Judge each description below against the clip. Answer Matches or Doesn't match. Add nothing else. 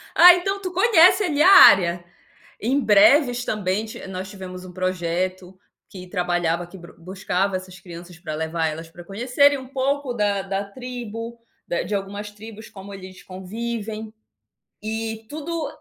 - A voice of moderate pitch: Doesn't match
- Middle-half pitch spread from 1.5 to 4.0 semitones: Doesn't match